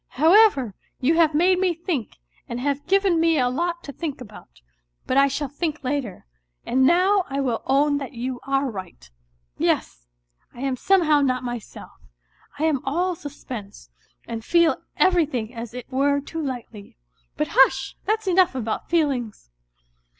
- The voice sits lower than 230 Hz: No, very high, 280 Hz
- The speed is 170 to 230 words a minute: No, average, 155 wpm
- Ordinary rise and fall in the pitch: Yes, average, 5.0 semitones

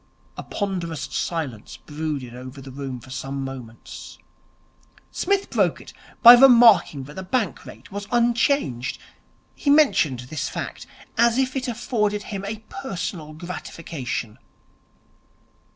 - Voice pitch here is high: No, medium, 170 Hz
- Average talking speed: No, slow, 125 wpm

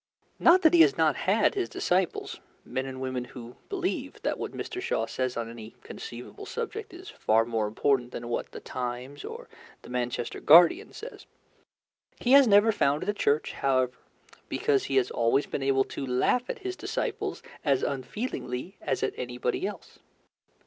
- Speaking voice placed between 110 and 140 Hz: Yes, low, 135 Hz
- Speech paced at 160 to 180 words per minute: Yes, average, 170 wpm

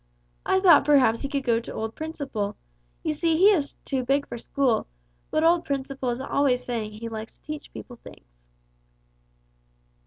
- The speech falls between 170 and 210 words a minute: Yes, average, 175 wpm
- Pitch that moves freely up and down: No, average, 4.7 semitones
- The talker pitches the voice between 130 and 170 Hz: No, very high, 270 Hz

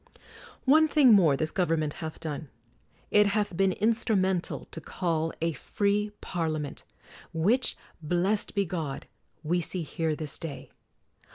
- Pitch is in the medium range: Yes, medium, 175 Hz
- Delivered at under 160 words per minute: Yes, slow, 135 wpm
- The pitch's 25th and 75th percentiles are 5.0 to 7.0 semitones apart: No, average, 4.4 semitones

